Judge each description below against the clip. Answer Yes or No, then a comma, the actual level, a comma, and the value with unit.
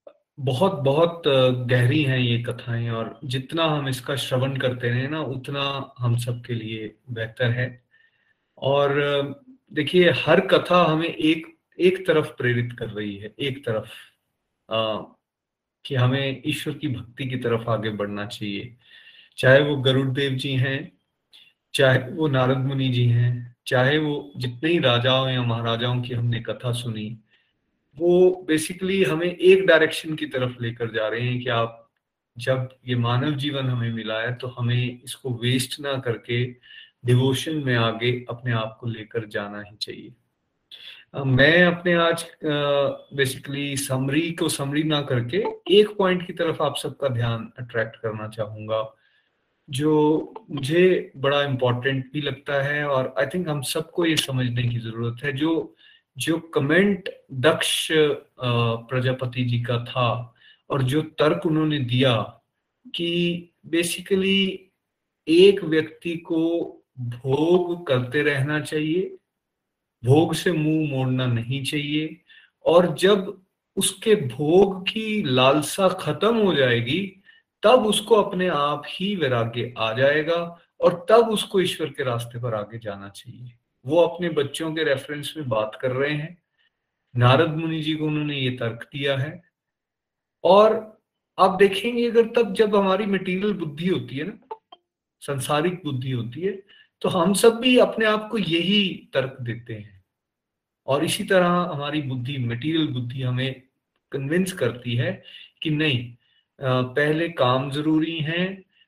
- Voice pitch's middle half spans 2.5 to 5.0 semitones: No, wide, 5.5 semitones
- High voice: No, medium, 140 Hz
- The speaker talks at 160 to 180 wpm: No, average, 145 wpm